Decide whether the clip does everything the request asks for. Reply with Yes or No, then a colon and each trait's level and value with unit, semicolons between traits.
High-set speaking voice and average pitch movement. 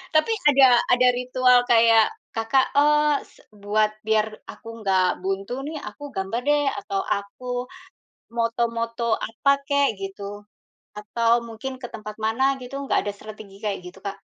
Yes: high, 230 Hz; average, 3.6 semitones